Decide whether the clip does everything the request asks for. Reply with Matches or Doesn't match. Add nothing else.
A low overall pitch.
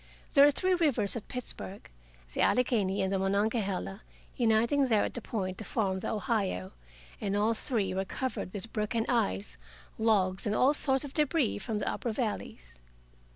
Doesn't match